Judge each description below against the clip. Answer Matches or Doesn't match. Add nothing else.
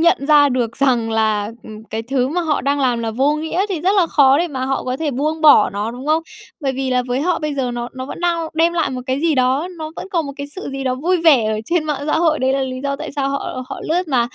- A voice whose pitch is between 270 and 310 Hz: Matches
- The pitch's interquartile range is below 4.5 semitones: Matches